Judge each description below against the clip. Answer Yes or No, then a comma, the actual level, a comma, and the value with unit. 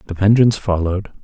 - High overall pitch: No, low, 100 Hz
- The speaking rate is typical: Yes, average, 145 wpm